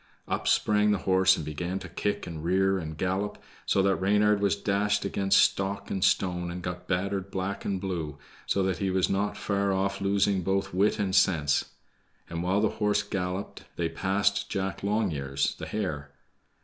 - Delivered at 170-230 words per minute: Yes, average, 180 wpm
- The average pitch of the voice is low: Yes, very low, 95 Hz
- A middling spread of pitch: No, narrow, 2.0 semitones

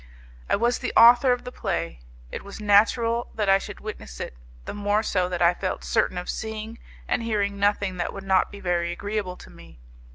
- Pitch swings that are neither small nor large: Yes, average, 3.3 semitones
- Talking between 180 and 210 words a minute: Yes, fast, 205 wpm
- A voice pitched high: Yes, high, 200 Hz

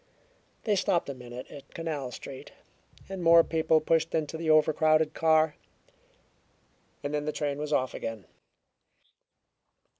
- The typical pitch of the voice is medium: Yes, medium, 155 Hz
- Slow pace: Yes, slow, 130 wpm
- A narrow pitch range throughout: Yes, narrow, 2.3 semitones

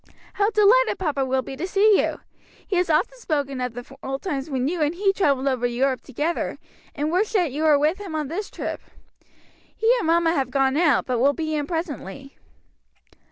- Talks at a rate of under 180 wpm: No, fast, 205 wpm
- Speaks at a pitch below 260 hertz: No, very high, 305 Hz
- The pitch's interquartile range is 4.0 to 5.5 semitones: Yes, average, 5.1 semitones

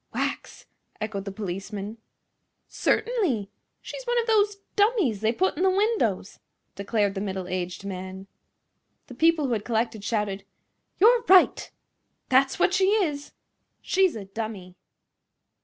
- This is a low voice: No, high, 230 Hz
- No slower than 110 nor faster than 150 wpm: Yes, slow, 135 wpm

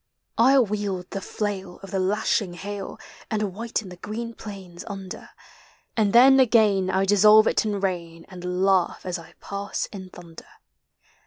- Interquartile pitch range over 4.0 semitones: No, narrow, 2.6 semitones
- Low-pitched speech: No, high, 195 Hz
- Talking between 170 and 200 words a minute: No, average, 155 wpm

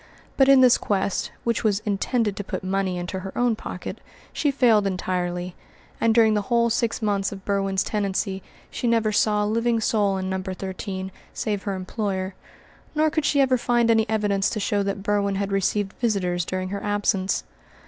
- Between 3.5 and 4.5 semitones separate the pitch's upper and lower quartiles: No, average, 2.9 semitones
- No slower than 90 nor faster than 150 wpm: No, average, 185 wpm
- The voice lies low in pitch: No, high, 205 Hz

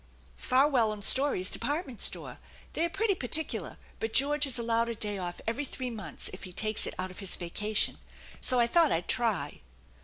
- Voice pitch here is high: Yes, high, 235 Hz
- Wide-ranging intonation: No, average, 5.0 semitones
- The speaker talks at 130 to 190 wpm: No, fast, 205 wpm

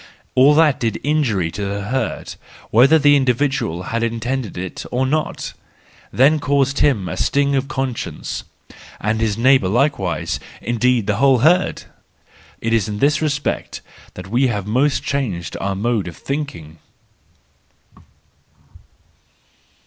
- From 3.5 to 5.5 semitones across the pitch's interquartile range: Yes, average, 5.2 semitones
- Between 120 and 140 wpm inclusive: Yes, slow, 135 wpm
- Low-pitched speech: Yes, low, 125 Hz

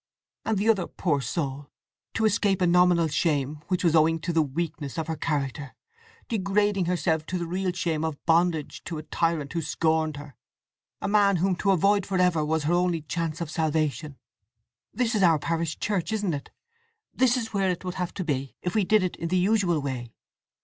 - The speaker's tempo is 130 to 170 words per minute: No, average, 195 wpm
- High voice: No, medium, 170 Hz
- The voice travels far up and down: No, average, 3.4 semitones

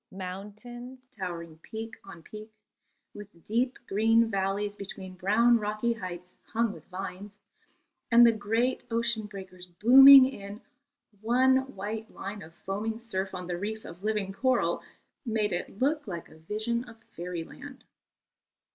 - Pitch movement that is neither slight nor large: Yes, average, 3.6 semitones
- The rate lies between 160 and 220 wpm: No, average, 140 wpm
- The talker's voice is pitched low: No, high, 210 Hz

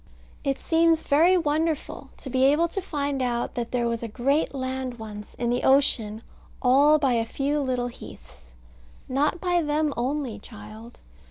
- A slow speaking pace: No, average, 165 wpm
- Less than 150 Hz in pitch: No, very high, 265 Hz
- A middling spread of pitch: Yes, average, 3.9 semitones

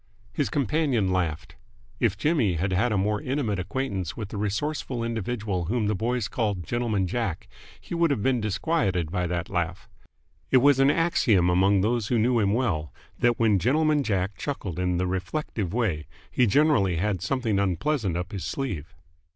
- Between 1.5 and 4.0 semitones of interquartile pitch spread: No, average, 5.3 semitones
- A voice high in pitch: No, low, 105 Hz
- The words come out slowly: No, average, 175 wpm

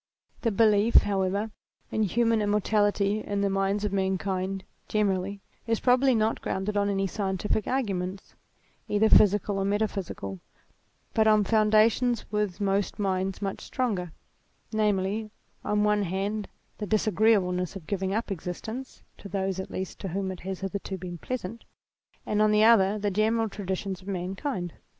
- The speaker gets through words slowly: No, average, 150 wpm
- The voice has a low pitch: No, high, 200 Hz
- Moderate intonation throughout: No, narrow, 2.1 semitones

